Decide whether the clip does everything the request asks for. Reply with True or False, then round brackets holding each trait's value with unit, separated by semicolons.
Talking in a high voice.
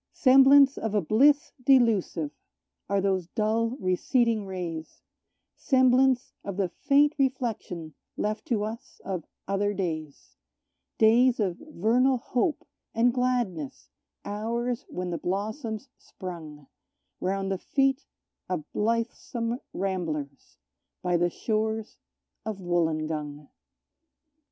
True (215 Hz)